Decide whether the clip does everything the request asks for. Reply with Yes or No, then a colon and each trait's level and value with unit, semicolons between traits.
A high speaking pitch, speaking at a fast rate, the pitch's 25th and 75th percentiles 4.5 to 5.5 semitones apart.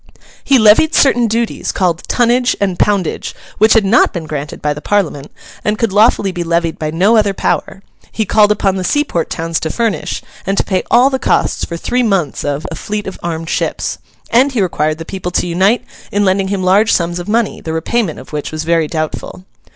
Yes: high, 195 Hz; fast, 210 wpm; average, 4.8 semitones